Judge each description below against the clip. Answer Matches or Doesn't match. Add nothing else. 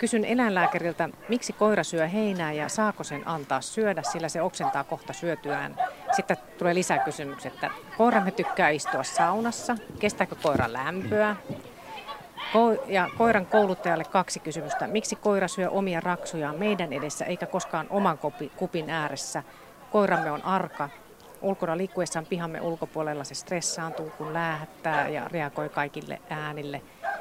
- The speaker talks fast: Doesn't match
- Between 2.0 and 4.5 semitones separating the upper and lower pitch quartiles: Doesn't match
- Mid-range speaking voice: Matches